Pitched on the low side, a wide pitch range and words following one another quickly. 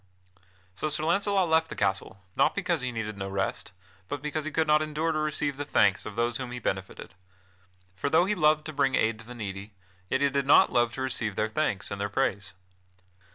Yes: low, 130 Hz; wide, 6.4 semitones; fast, 220 wpm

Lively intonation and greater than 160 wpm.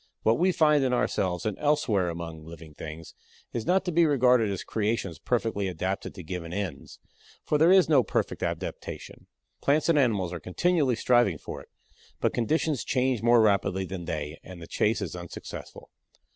Yes: wide, 7.4 semitones; average, 175 wpm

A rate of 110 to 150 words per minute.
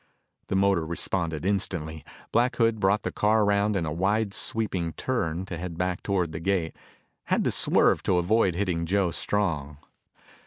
No: average, 165 wpm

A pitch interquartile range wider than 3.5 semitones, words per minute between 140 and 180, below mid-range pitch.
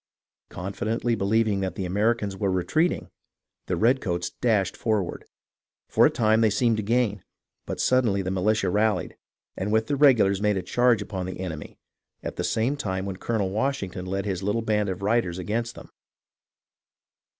No: average, 3.2 semitones; average, 165 wpm; low, 105 Hz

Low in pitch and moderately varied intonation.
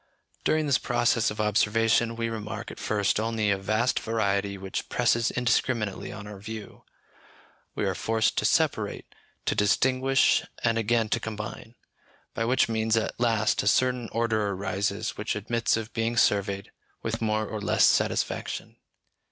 No: low, 110 Hz; narrow, 1.9 semitones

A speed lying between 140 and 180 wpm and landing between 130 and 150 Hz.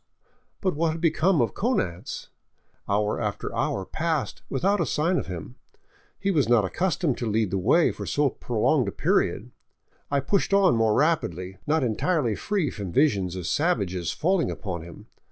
Yes: average, 170 wpm; low, 135 Hz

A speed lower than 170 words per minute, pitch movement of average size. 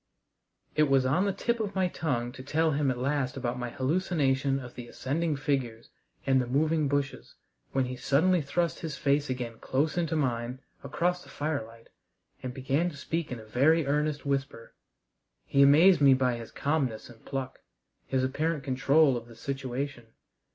No: average, 175 wpm; average, 3.3 semitones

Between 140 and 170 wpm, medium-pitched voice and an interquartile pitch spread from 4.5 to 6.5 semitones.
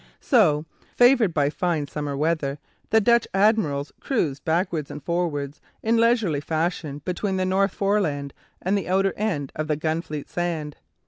Yes: average, 150 wpm; medium, 170 Hz; average, 5.0 semitones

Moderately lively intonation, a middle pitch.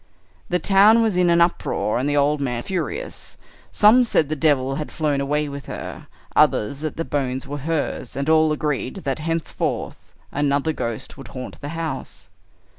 Yes: average, 3.2 semitones; medium, 150 Hz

